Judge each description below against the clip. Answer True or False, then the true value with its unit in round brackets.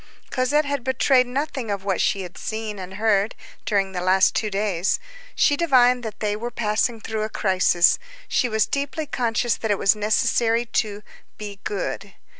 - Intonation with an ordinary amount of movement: True (3.5 semitones)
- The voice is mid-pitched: False (220 Hz)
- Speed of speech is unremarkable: True (175 wpm)